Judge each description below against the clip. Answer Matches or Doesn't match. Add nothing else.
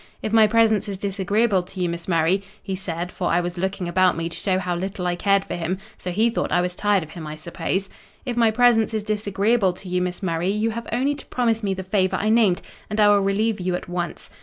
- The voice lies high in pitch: Matches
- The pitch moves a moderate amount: Matches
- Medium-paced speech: Doesn't match